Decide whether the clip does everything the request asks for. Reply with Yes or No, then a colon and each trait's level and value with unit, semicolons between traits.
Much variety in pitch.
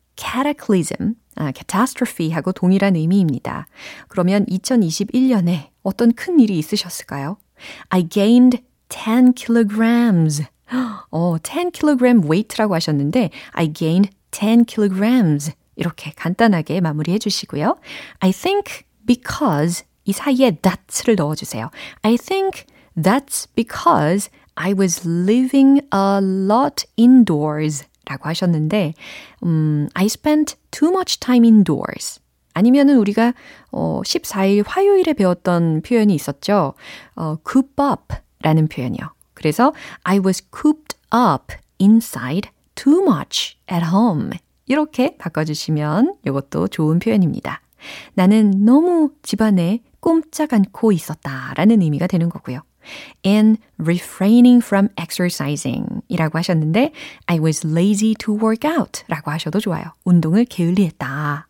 Yes: wide, 6.7 semitones